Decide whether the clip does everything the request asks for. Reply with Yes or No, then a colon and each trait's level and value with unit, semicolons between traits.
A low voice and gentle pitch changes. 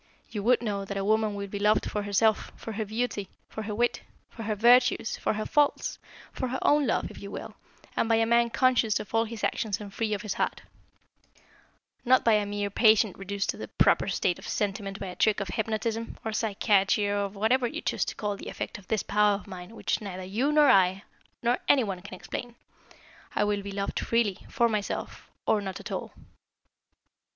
No: high, 210 Hz; narrow, 2.3 semitones